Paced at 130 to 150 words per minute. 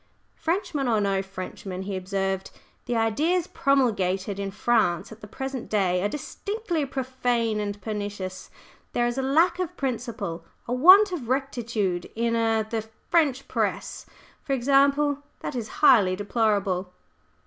Yes: average, 140 wpm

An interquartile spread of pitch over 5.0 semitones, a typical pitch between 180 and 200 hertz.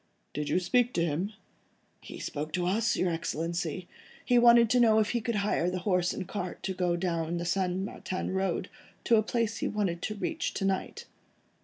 No: average, 3.9 semitones; medium, 185 Hz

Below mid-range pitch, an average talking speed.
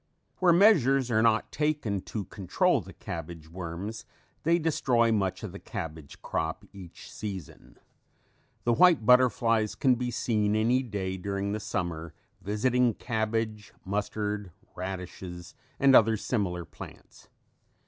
No: low, 105 Hz; slow, 130 wpm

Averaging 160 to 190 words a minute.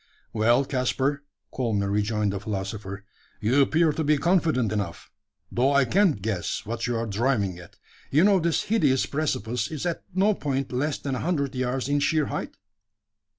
Yes: average, 170 wpm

